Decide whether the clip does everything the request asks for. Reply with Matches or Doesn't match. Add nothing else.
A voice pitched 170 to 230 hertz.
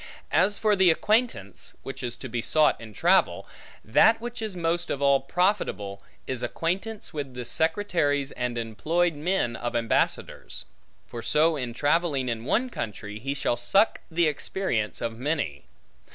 Doesn't match